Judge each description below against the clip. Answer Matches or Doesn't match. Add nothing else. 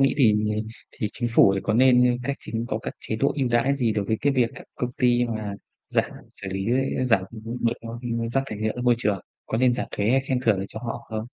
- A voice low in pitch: Matches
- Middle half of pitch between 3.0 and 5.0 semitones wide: Doesn't match